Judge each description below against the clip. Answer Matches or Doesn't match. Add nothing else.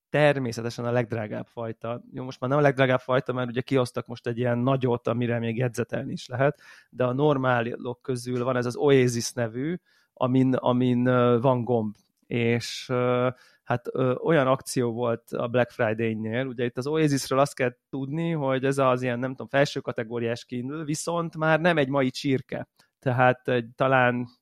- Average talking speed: Doesn't match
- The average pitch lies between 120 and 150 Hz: Matches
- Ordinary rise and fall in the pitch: Doesn't match